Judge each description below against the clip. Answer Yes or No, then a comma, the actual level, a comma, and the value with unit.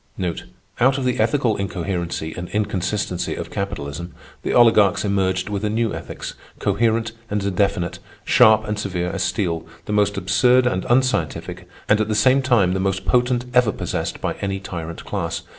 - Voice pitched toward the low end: Yes, low, 100 Hz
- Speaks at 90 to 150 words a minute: No, average, 165 wpm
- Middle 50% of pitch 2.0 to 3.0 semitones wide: No, average, 3.4 semitones